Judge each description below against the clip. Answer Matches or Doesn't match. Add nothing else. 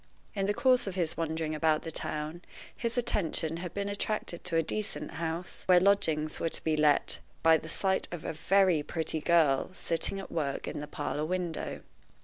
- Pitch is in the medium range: Matches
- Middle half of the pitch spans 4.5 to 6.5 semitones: Doesn't match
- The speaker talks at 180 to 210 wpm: Matches